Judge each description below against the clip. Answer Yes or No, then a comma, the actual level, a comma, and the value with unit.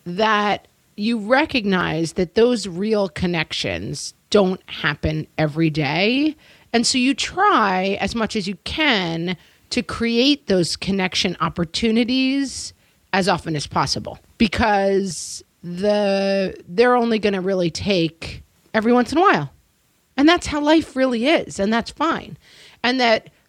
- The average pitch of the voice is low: No, high, 205 Hz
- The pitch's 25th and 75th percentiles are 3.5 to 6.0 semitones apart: Yes, average, 4.9 semitones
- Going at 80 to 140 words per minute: Yes, slow, 135 wpm